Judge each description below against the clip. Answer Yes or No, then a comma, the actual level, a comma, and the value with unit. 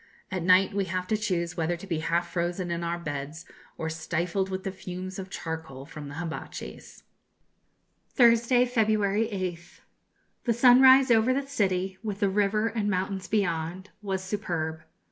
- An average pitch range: Yes, average, 3.6 semitones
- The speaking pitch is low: No, high, 190 Hz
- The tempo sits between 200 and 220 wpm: No, average, 160 wpm